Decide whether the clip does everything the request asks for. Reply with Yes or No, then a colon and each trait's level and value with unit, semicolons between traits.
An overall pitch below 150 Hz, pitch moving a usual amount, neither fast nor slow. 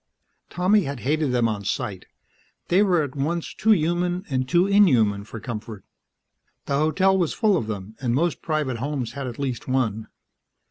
No: medium, 140 Hz; wide, 6.7 semitones; average, 175 wpm